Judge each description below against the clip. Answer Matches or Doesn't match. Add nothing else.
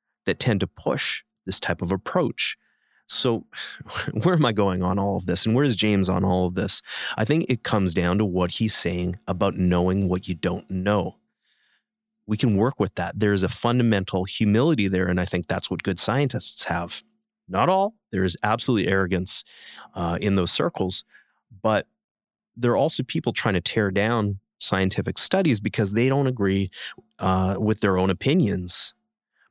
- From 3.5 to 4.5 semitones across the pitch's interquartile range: Matches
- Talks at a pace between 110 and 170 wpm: Doesn't match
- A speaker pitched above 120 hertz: Doesn't match